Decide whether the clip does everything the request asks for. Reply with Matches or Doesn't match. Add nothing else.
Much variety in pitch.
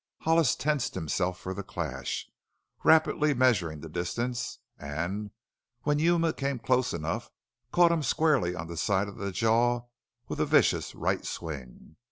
Matches